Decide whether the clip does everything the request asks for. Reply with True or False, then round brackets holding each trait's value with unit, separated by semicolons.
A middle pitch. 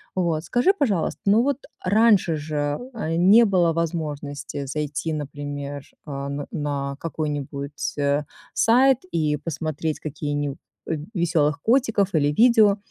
True (155 Hz)